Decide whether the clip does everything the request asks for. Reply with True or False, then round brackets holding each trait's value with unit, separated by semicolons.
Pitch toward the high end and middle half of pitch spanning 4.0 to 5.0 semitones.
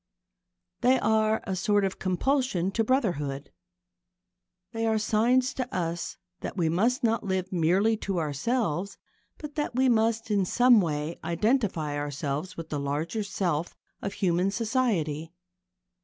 False (195 Hz; 5.4 semitones)